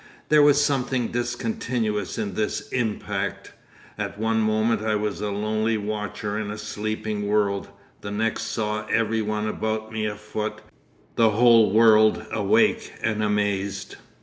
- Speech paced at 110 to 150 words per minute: Yes, average, 140 wpm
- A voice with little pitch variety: Yes, narrow, 1.3 semitones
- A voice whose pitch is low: Yes, low, 110 Hz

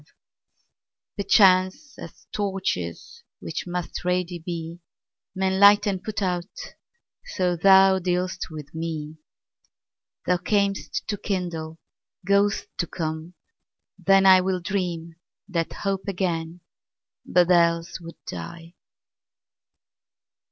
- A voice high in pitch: No, medium, 180 Hz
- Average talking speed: No, slow, 95 wpm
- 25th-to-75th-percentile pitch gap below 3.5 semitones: Yes, narrow, 2.5 semitones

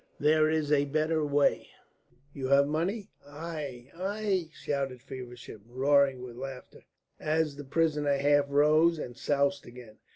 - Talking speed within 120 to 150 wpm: Yes, slow, 135 wpm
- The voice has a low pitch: No, medium, 145 Hz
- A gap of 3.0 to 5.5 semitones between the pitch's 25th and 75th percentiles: No, narrow, 2.5 semitones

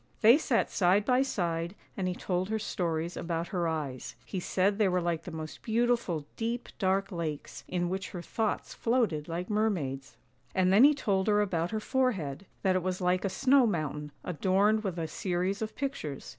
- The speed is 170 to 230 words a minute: Yes, average, 190 wpm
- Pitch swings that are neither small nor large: Yes, average, 4.2 semitones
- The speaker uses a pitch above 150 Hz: Yes, medium, 185 Hz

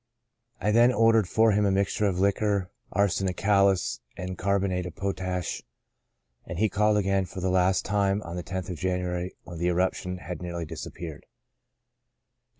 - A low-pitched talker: Yes, very low, 95 Hz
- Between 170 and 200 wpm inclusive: No, average, 160 wpm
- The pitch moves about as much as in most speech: No, narrow, 2.0 semitones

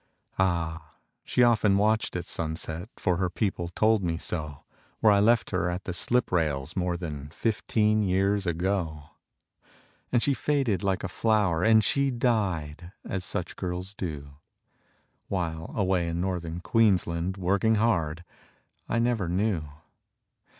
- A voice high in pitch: No, very low, 95 Hz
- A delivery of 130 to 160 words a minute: Yes, average, 140 wpm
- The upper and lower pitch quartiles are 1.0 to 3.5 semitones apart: No, average, 4.2 semitones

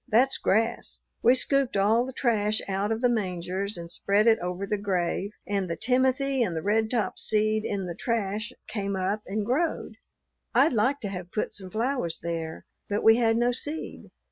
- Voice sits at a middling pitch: No, high, 215 Hz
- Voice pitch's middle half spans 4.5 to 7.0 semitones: No, average, 3.7 semitones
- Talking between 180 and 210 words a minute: Yes, average, 185 wpm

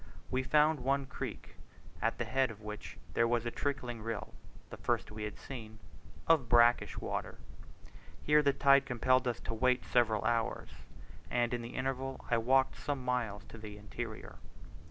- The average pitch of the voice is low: Yes, low, 120 Hz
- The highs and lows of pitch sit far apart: No, average, 2.9 semitones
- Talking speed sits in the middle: Yes, average, 170 wpm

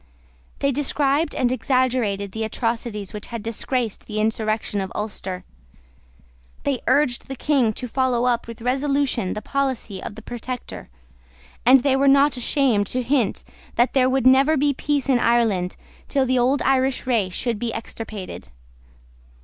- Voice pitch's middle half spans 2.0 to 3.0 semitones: No, average, 3.4 semitones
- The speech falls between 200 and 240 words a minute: No, average, 155 wpm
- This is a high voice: Yes, high, 245 Hz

